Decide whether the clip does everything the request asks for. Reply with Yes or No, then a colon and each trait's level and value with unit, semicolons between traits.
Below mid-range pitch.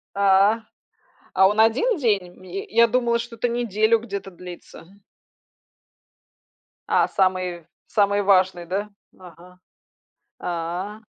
No: high, 200 Hz